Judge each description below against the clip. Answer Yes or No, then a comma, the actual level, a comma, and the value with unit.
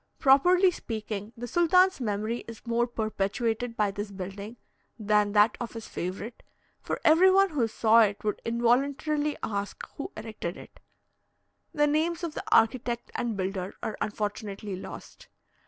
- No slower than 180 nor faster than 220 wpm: No, average, 145 wpm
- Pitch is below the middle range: No, high, 230 Hz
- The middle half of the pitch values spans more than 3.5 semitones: Yes, average, 5.0 semitones